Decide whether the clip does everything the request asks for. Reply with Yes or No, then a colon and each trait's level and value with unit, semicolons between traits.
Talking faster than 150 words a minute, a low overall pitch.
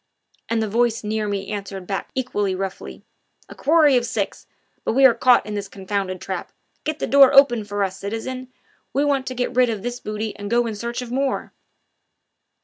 No: average, 200 wpm; high, 225 Hz